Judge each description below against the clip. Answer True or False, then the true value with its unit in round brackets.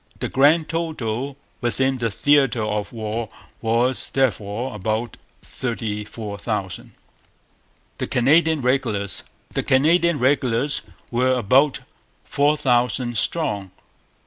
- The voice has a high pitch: False (125 Hz)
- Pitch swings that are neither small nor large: True (4.1 semitones)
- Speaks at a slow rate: True (105 wpm)